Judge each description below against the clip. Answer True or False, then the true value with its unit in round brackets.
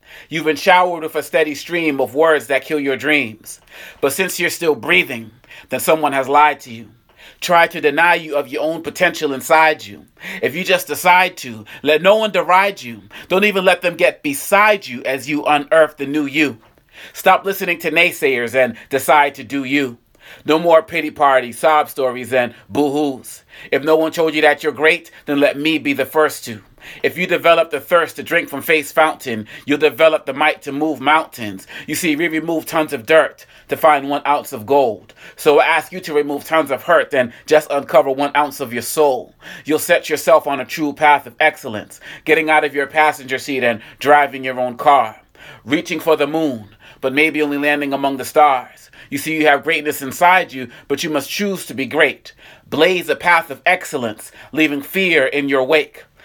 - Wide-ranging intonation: False (3.0 semitones)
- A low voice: False (150 Hz)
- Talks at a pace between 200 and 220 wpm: True (205 wpm)